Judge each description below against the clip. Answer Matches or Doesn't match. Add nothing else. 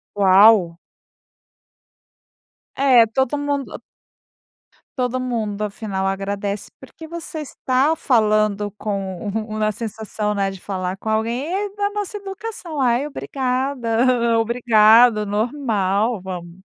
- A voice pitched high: Matches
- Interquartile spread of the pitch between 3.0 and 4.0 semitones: Doesn't match